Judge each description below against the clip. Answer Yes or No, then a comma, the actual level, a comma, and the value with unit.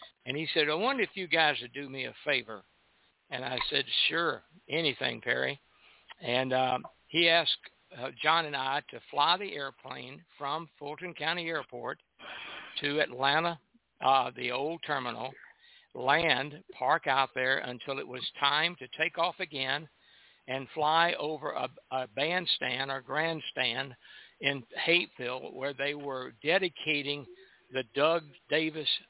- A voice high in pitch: No, medium, 145 Hz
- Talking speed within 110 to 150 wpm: Yes, average, 145 wpm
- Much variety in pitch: No, average, 3.7 semitones